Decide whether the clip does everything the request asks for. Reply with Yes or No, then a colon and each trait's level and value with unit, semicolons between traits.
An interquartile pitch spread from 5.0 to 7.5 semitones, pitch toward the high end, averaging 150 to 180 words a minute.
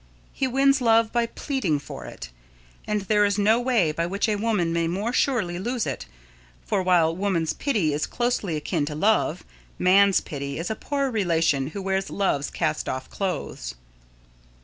Yes: wide, 5.6 semitones; high, 195 Hz; average, 170 wpm